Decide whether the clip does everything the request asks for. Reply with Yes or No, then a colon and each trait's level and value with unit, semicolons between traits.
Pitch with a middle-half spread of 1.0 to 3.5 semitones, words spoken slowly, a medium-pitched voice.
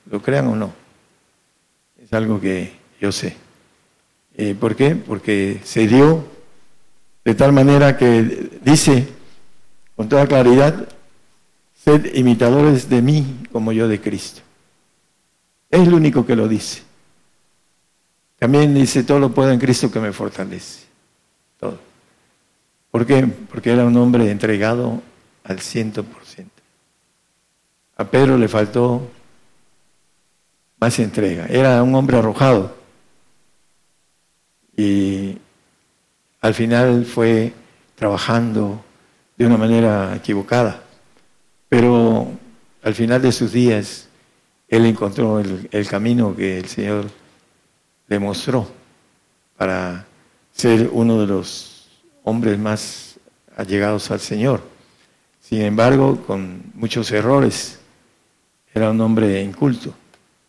No: average, 3.2 semitones; slow, 110 wpm; low, 115 Hz